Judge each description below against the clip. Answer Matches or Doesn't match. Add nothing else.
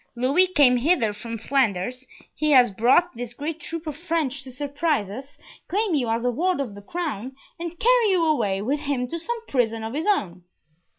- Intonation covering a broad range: Matches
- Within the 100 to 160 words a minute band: Doesn't match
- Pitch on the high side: Matches